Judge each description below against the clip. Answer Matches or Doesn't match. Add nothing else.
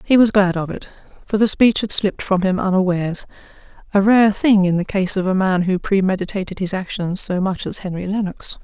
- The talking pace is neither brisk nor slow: Doesn't match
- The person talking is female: Matches